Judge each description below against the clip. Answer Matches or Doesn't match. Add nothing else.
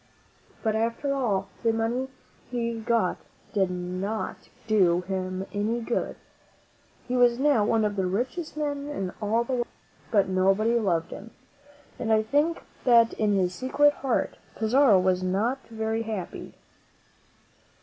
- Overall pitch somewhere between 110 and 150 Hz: Doesn't match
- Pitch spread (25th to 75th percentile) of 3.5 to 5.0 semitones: Matches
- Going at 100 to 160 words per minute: Matches